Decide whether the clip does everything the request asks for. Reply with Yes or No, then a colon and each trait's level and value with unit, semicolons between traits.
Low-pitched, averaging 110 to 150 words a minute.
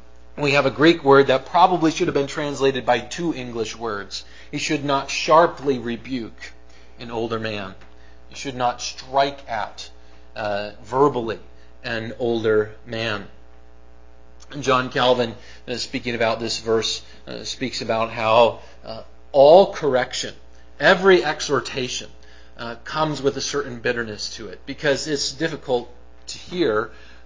Yes: low, 115 Hz; average, 140 wpm